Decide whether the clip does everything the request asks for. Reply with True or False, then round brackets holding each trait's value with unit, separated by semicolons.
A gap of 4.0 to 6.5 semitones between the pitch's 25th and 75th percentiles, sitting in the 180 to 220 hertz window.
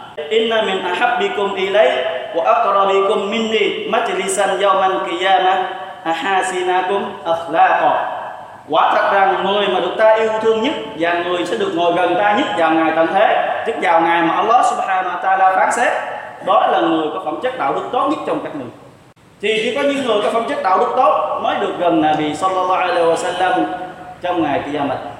False (3.3 semitones; 190 Hz)